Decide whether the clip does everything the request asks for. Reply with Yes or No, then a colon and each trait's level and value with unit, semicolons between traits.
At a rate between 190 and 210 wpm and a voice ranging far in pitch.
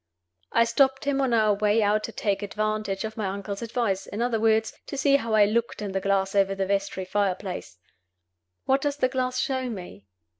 No: average, 200 wpm; average, 3.5 semitones